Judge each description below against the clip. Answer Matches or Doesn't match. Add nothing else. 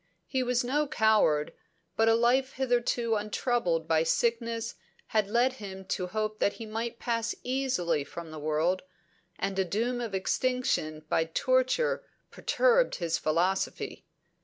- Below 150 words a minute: Matches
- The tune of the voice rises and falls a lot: Matches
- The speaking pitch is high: Matches